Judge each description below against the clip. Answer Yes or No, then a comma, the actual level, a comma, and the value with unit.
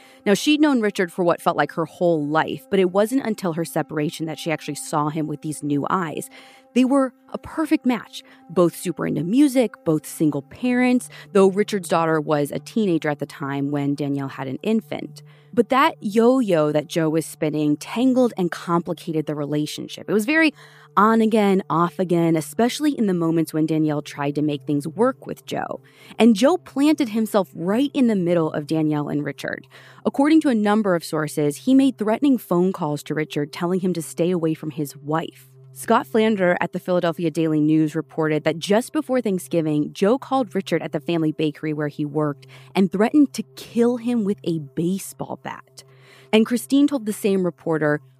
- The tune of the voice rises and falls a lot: Yes, wide, 6.5 semitones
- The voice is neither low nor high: Yes, medium, 170 Hz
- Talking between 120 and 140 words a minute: No, average, 195 wpm